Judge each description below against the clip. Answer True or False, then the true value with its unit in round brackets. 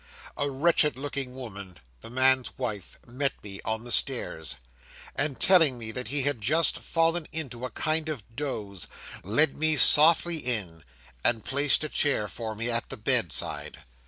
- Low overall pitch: True (130 Hz)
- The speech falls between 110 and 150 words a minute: False (160 wpm)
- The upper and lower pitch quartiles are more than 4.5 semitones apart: True (4.9 semitones)